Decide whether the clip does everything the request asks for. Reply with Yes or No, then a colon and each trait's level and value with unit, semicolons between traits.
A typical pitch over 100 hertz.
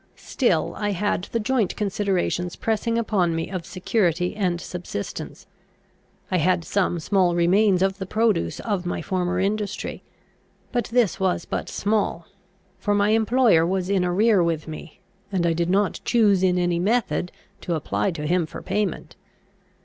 Yes: high, 190 Hz